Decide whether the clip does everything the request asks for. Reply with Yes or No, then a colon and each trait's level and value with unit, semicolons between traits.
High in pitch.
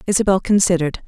No: medium, 180 Hz